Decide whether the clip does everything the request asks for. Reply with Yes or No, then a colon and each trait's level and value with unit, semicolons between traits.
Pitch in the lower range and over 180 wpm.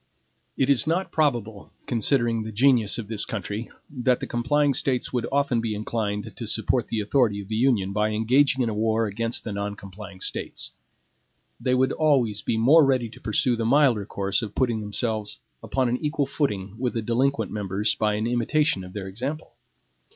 Yes: low, 115 Hz; average, 190 wpm